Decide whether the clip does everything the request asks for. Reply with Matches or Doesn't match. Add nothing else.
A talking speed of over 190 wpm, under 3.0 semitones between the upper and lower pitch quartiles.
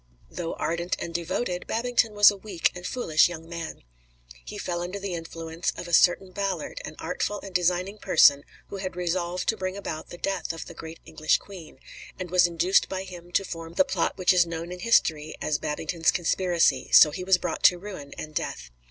Matches